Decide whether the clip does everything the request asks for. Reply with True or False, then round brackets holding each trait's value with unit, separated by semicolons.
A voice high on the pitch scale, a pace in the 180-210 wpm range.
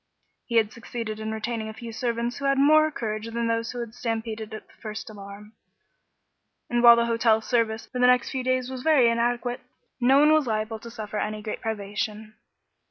True (230 Hz; 200 wpm)